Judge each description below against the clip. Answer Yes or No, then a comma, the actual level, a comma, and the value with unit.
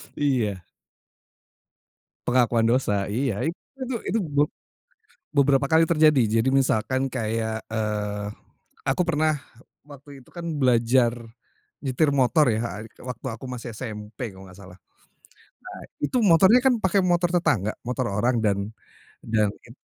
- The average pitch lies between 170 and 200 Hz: No, low, 125 Hz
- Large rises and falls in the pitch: No, average, 5.0 semitones